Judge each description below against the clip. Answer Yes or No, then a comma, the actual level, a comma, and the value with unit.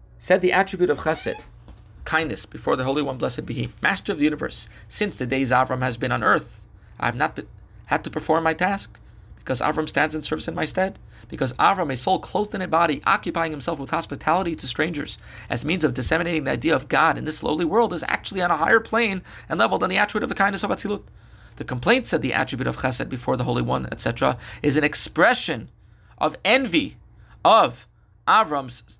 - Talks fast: Yes, fast, 215 wpm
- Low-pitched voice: No, medium, 150 Hz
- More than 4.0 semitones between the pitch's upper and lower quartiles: Yes, average, 5.0 semitones